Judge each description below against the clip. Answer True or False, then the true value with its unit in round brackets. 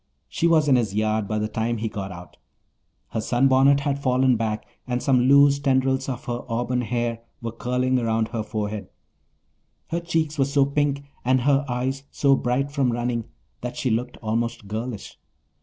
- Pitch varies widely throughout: False (3.2 semitones)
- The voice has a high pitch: False (125 Hz)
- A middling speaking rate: True (175 wpm)